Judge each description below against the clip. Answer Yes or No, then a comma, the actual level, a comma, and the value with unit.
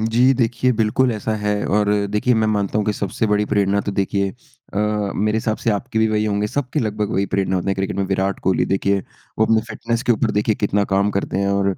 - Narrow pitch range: Yes, narrow, 1.9 semitones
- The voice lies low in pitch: Yes, low, 105 Hz